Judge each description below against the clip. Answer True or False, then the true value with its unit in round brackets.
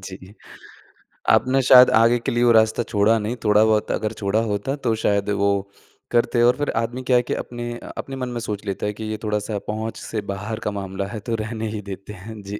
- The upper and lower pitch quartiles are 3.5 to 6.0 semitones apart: False (2.5 semitones)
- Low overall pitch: True (110 Hz)